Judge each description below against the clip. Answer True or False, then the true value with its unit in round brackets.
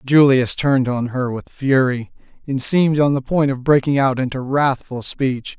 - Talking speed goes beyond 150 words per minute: True (185 wpm)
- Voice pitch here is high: False (135 Hz)